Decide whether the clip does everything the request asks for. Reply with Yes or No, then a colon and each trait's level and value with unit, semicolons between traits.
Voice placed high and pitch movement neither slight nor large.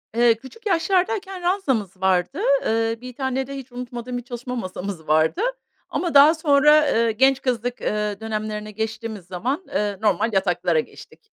Yes: high, 235 Hz; average, 4.8 semitones